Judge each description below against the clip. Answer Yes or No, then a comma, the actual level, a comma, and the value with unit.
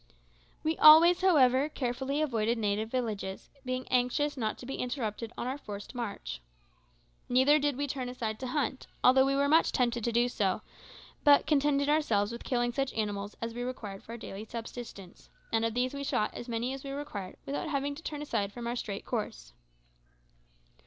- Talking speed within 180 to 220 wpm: Yes, average, 185 wpm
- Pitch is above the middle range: Yes, very high, 250 Hz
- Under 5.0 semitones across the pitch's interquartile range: Yes, average, 3.9 semitones